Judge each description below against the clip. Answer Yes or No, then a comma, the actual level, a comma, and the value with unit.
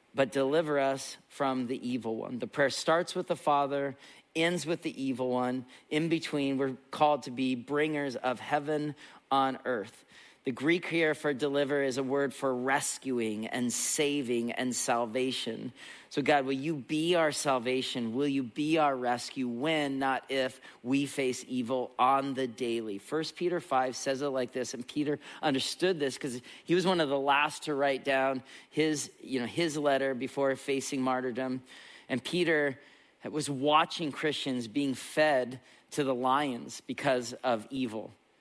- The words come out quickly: No, average, 165 wpm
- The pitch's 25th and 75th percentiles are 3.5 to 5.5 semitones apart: No, narrow, 2.5 semitones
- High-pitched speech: No, low, 135 Hz